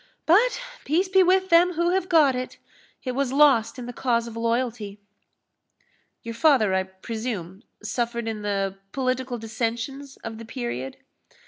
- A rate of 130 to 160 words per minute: Yes, average, 150 wpm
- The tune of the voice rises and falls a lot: No, average, 4.1 semitones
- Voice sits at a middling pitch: No, high, 245 Hz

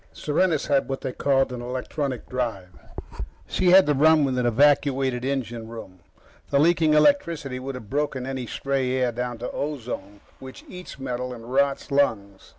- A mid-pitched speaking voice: No, low, 130 Hz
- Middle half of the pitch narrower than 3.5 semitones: Yes, average, 2.8 semitones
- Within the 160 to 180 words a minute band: Yes, average, 165 wpm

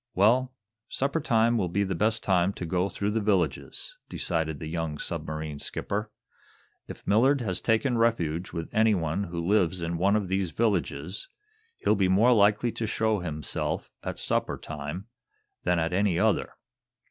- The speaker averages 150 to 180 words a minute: Yes, average, 160 wpm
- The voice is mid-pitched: No, very low, 95 Hz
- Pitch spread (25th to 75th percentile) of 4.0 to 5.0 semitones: Yes, average, 4.6 semitones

